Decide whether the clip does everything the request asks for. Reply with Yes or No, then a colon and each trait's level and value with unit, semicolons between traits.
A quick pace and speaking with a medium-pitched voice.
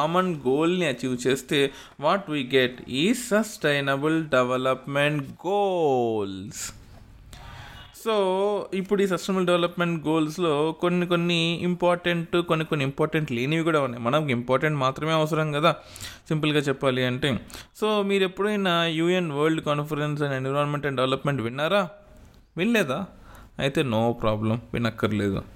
No: average, 115 wpm; medium, 150 Hz